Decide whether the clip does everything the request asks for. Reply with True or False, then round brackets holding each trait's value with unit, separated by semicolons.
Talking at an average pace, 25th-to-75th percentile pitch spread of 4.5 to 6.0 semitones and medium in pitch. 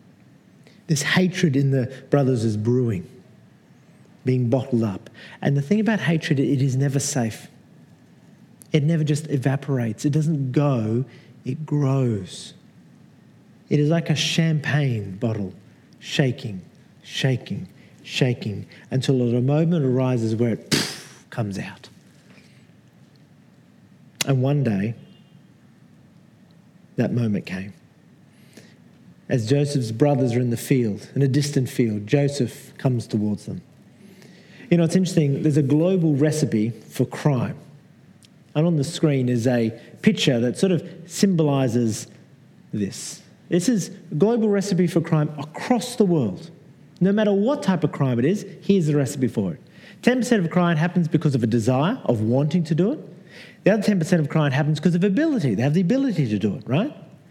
True (150 wpm; 5.3 semitones; 145 Hz)